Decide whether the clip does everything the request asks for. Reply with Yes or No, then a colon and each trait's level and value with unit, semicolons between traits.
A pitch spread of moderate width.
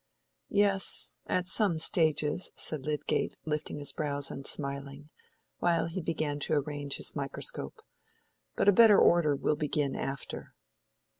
Yes: average, 3.1 semitones